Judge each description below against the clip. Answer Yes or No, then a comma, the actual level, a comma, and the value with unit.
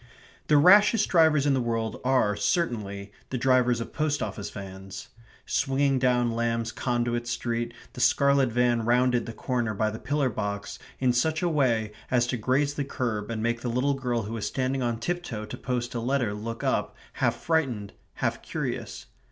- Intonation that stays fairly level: No, average, 3.0 semitones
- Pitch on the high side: No, low, 120 Hz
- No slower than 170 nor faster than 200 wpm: Yes, average, 180 wpm